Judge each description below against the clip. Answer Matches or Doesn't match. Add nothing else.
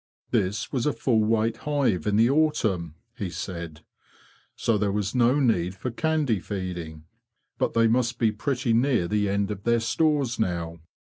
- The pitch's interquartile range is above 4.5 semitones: Matches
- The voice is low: Matches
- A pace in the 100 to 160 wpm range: Doesn't match